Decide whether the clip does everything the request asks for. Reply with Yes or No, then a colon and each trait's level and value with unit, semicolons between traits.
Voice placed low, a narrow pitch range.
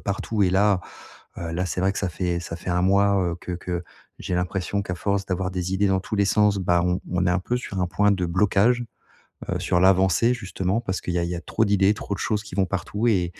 Yes: very low, 95 Hz; narrow, 2.1 semitones